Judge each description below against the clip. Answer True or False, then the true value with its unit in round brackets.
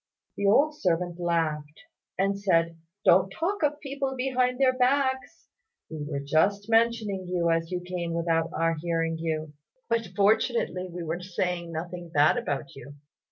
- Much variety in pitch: True (5.7 semitones)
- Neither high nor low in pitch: True (180 Hz)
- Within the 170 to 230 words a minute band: False (155 wpm)